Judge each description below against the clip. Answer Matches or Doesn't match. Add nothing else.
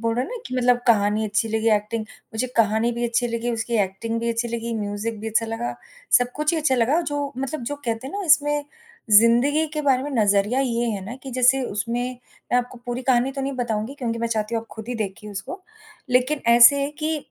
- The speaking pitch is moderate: Doesn't match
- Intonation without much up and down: Doesn't match